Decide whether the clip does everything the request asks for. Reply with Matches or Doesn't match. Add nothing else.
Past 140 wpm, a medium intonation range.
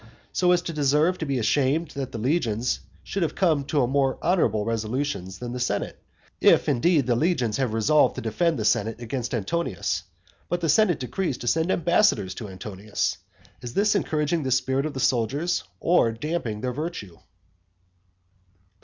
Doesn't match